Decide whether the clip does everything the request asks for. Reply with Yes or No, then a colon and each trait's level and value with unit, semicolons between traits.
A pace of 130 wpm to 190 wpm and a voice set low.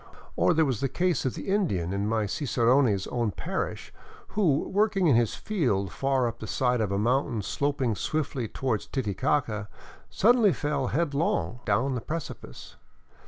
Yes: average, 160 wpm; low, 130 Hz